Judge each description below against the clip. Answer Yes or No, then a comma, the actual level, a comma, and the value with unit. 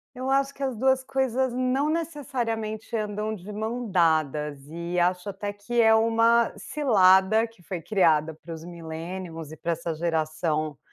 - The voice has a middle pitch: No, high, 205 Hz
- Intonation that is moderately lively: No, wide, 6.2 semitones